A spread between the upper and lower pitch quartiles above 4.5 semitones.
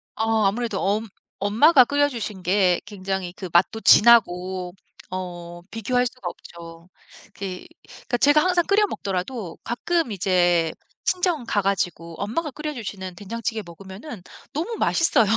Yes: average, 5.3 semitones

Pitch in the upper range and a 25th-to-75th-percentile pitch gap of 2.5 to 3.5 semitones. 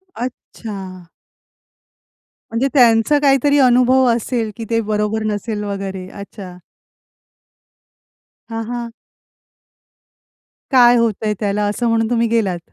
Yes: high, 225 Hz; average, 2.8 semitones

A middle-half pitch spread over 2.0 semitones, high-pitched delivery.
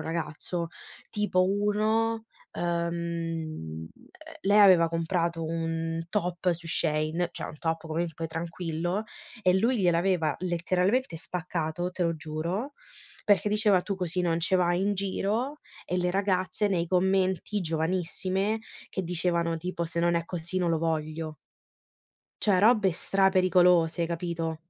No: narrow, 2.5 semitones; medium, 175 Hz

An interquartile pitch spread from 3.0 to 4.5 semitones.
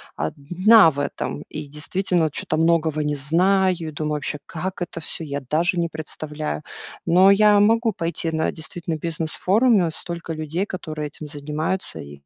Yes: average, 3.3 semitones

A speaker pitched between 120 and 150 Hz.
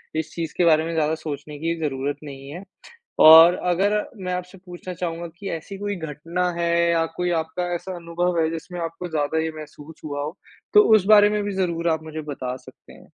No: medium, 165 Hz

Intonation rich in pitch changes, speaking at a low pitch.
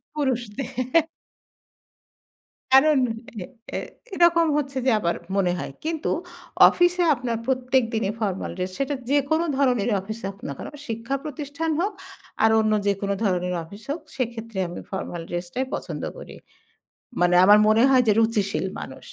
No: wide, 5.8 semitones; high, 235 Hz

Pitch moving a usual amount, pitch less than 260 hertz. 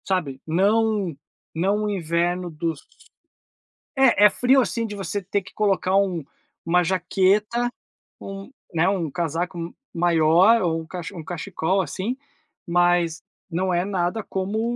Yes: average, 3.2 semitones; medium, 185 Hz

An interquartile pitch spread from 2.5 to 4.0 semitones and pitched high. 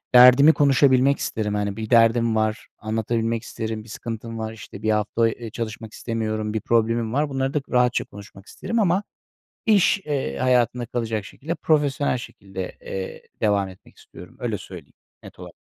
No: average, 2.8 semitones; low, 115 Hz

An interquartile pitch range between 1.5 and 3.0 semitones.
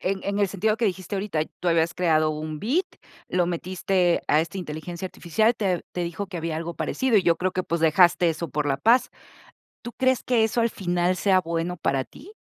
No: average, 3.4 semitones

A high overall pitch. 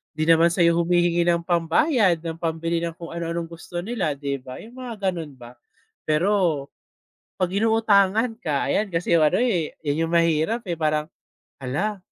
No: medium, 170 Hz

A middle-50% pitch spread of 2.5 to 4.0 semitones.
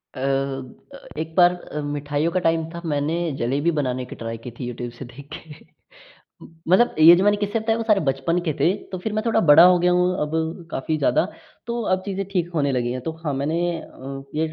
No: average, 4.7 semitones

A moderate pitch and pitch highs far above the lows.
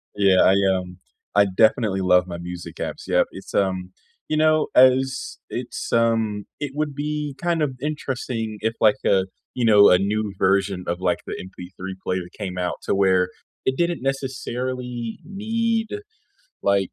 No: low, 110 Hz; wide, 6.3 semitones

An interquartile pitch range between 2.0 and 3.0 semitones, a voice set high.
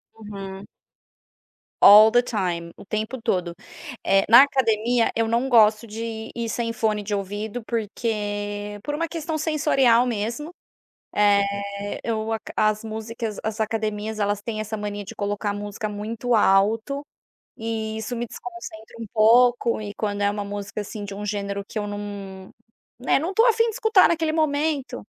Yes: narrow, 2.6 semitones; high, 220 Hz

